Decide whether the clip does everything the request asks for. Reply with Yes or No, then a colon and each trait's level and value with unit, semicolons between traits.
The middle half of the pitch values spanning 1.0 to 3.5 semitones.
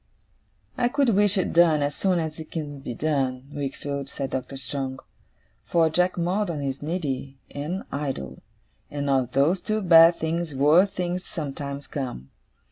No: average, 4.1 semitones